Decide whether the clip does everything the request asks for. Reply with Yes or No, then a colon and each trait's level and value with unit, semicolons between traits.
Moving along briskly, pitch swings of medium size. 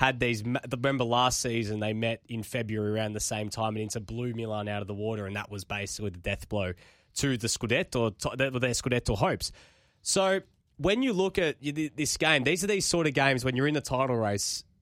Yes: fast, 215 wpm; average, 4.4 semitones